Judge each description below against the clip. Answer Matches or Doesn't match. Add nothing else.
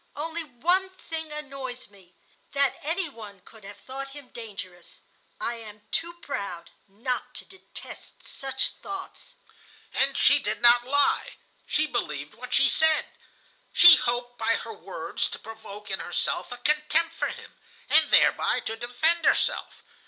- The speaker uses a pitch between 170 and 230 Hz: Doesn't match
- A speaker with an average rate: Matches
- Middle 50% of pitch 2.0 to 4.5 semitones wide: Doesn't match